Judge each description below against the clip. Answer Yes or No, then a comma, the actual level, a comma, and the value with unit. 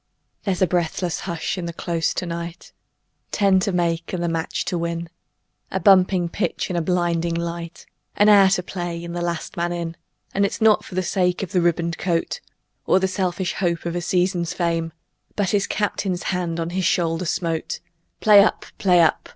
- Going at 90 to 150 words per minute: No, average, 195 wpm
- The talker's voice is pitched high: No, medium, 175 Hz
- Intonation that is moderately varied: No, narrow, 1.8 semitones